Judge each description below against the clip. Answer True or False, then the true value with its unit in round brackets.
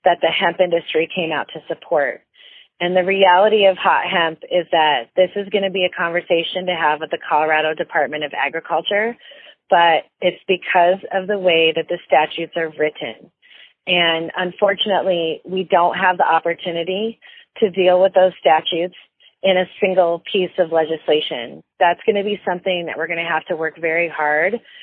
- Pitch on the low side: False (175 Hz)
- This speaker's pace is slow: False (170 wpm)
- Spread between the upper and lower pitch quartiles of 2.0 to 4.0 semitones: True (2.6 semitones)